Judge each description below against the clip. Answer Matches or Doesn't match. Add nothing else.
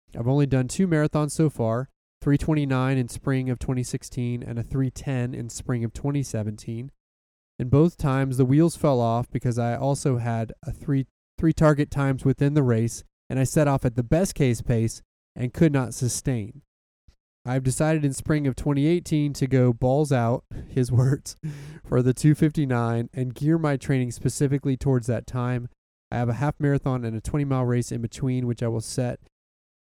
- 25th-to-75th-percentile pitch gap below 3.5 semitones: Matches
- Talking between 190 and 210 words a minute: Matches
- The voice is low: Matches